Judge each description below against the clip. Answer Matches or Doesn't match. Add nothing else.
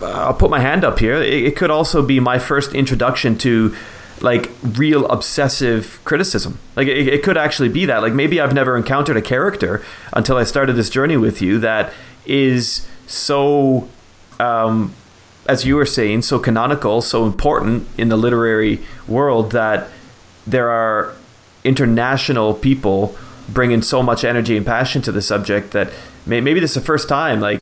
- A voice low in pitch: Matches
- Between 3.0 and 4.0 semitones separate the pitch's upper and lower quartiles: Matches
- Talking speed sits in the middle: Matches